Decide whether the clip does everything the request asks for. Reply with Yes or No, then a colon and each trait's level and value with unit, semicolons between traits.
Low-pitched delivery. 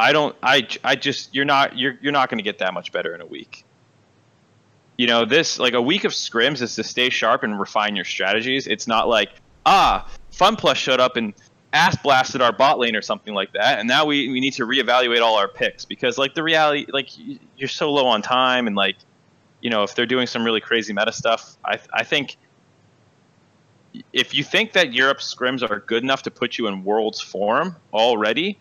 Yes: low, 130 Hz